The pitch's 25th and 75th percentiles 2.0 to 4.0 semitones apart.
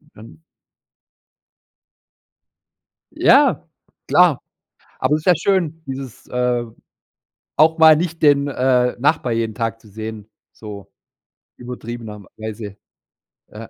No: average, 5.1 semitones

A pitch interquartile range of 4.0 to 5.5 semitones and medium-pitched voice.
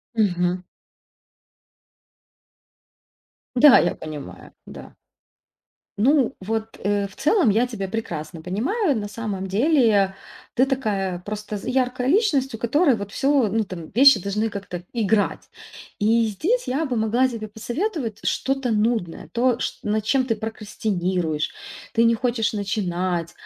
No: average, 4.5 semitones; high, 220 Hz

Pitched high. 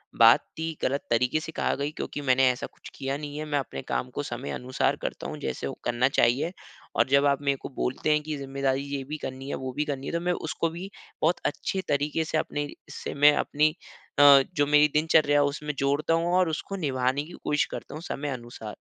No: medium, 145 Hz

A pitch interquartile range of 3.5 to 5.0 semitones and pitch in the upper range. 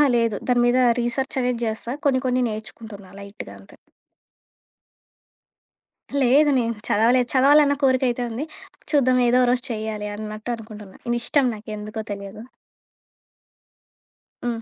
No: average, 3.0 semitones; high, 235 Hz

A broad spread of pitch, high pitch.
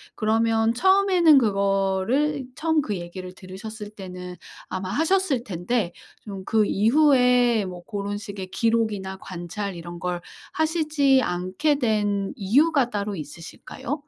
Yes: wide, 5.9 semitones; high, 210 Hz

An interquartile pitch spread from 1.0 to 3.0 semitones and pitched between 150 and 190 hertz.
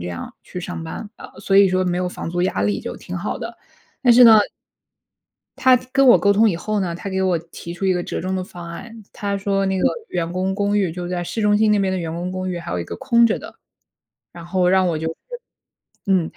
Yes: average, 2.7 semitones; medium, 185 Hz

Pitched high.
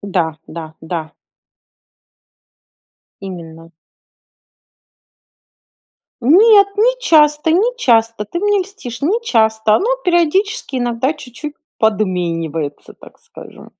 Yes: high, 245 Hz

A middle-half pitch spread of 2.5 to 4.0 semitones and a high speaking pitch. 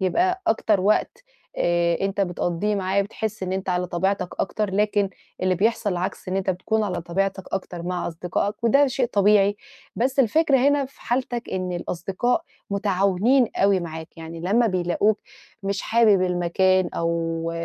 Yes: average, 3.4 semitones; high, 195 Hz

